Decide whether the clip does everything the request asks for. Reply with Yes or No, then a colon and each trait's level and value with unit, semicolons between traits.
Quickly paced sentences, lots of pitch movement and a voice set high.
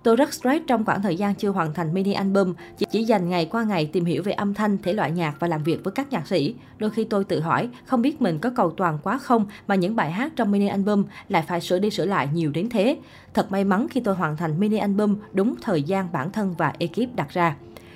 No: fast, 265 wpm; average, 3.9 semitones; high, 195 Hz